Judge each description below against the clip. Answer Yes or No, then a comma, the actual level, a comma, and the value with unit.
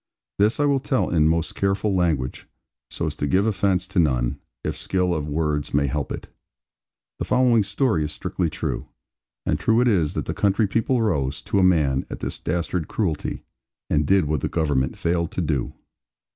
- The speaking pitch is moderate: No, very low, 85 Hz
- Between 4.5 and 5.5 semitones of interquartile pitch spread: Yes, average, 5.1 semitones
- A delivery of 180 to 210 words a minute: Yes, average, 195 wpm